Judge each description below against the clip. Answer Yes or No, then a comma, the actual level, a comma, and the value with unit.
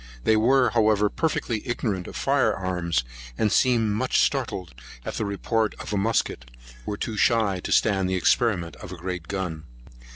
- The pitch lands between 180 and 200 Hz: No, low, 105 Hz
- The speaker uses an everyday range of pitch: Yes, average, 3.6 semitones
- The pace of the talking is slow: No, average, 170 wpm